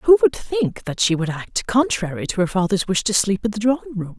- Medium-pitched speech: No, high, 220 Hz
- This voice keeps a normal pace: No, fast, 260 wpm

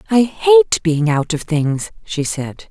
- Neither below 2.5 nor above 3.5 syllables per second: Yes, 3.4 syllables/s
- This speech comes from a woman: Yes, female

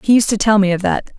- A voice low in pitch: No, high, 210 Hz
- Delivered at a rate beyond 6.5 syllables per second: Yes, 6.7 syllables/s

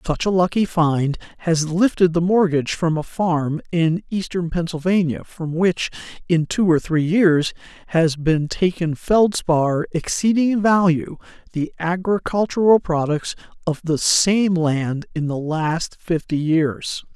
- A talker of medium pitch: Yes, medium, 170 Hz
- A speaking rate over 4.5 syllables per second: No, 4.0 syllables/s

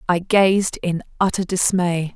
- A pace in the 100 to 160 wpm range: Yes, average, 140 wpm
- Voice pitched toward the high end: No, medium, 180 Hz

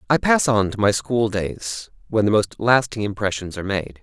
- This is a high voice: No, low, 105 Hz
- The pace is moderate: No, fast, 210 wpm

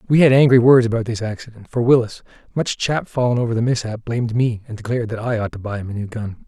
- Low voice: Yes, low, 115 Hz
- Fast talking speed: Yes, fast, 250 wpm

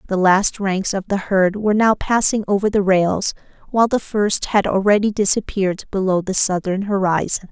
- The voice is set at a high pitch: Yes, high, 195 Hz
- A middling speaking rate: Yes, average, 175 wpm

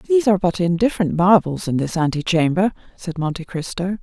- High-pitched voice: No, medium, 180 Hz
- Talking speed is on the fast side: No, average, 180 wpm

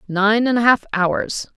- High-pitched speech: Yes, high, 215 Hz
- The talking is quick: No, average, 190 wpm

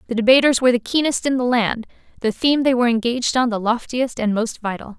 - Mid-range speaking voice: No, high, 240 Hz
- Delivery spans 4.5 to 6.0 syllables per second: No, 6.5 syllables/s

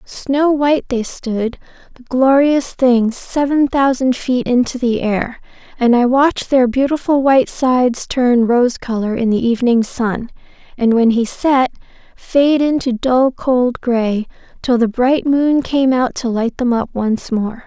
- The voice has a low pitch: No, very high, 250 Hz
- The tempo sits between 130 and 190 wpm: Yes, average, 165 wpm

